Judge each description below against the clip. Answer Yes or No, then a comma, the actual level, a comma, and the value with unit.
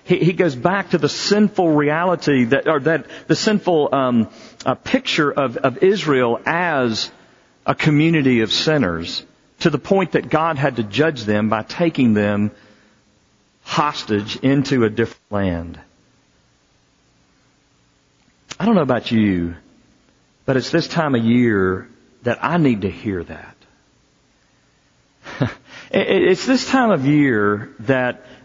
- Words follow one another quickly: No, slow, 135 wpm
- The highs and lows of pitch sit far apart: Yes, wide, 7.2 semitones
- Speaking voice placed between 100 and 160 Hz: Yes, low, 135 Hz